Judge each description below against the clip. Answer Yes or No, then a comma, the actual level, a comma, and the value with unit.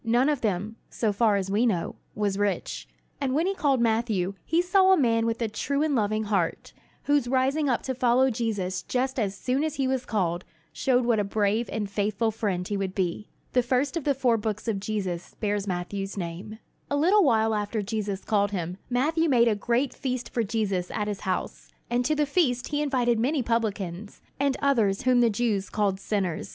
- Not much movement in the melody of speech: No, average, 4.3 semitones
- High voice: Yes, high, 225 Hz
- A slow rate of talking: No, fast, 205 wpm